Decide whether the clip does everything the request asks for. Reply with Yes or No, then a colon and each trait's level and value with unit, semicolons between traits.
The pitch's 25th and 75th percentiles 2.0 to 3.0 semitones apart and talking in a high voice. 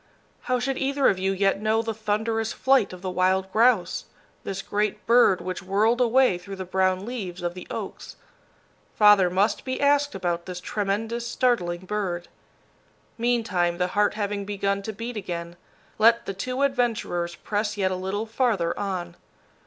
No: average, 3.7 semitones; high, 205 Hz